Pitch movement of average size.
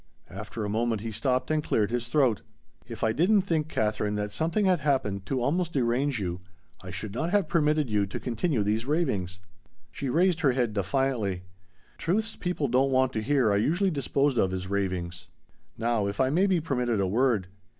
No: wide, 6.5 semitones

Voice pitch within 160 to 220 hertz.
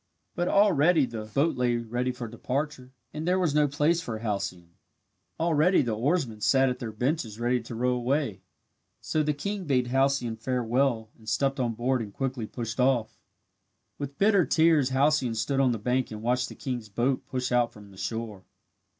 No: low, 125 Hz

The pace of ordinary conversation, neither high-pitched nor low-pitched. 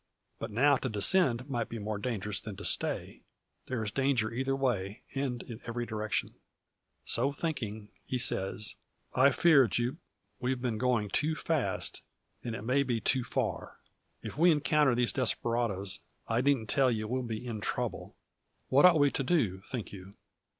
No: average, 170 wpm; low, 120 Hz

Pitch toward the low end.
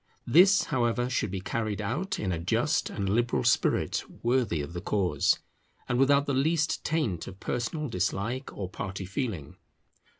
Yes: low, 115 Hz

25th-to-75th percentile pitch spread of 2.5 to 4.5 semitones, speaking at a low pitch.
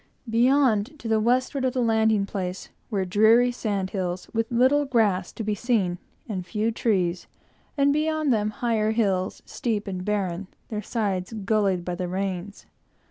No: average, 3.9 semitones; high, 215 Hz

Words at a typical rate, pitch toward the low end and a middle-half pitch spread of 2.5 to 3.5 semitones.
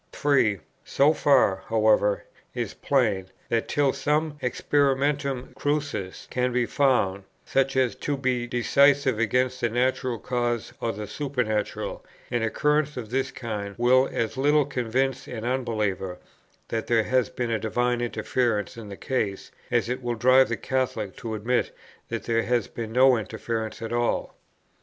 Yes: average, 150 wpm; low, 120 Hz; average, 2.9 semitones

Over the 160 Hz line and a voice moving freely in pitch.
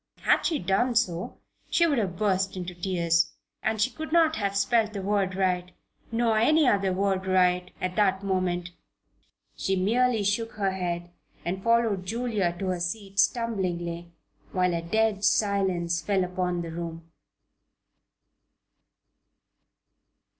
No: high, 190 Hz; average, 3.4 semitones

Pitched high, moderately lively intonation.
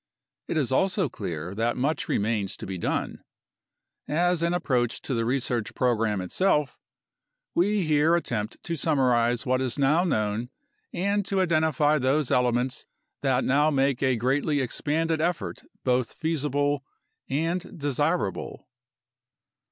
No: low, 135 Hz; average, 4.8 semitones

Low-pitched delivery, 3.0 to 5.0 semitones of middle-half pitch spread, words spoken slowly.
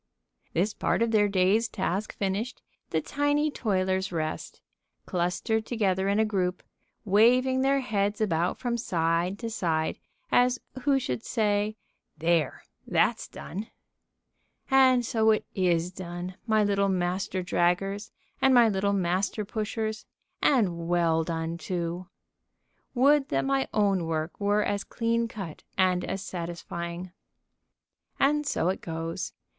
No: high, 195 Hz; average, 4.2 semitones; slow, 130 wpm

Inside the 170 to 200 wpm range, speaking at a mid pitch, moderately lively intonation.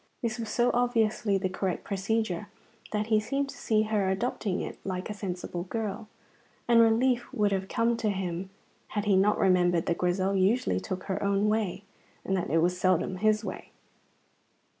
No: average, 180 wpm; high, 205 Hz; average, 3.0 semitones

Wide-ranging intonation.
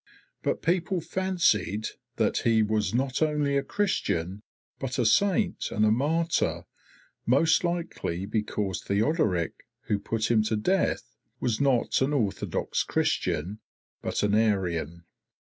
Yes: wide, 7.4 semitones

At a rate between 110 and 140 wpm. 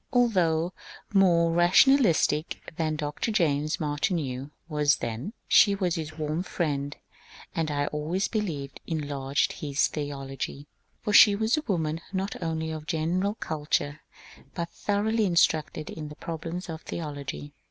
Yes: slow, 135 wpm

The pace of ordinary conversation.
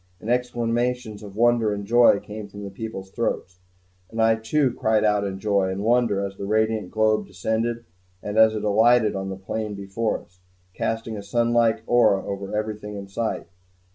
Yes: average, 180 wpm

